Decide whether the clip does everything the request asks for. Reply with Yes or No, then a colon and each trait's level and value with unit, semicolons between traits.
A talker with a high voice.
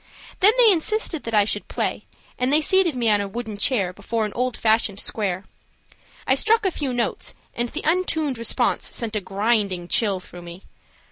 Yes: high, 230 Hz